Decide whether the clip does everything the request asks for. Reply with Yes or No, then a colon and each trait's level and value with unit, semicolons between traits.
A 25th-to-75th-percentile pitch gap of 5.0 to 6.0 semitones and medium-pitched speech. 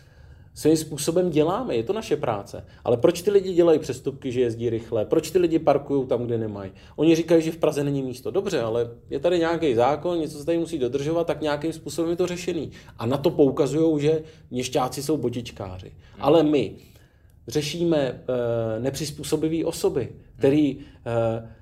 Yes: average, 5.3 semitones; medium, 145 Hz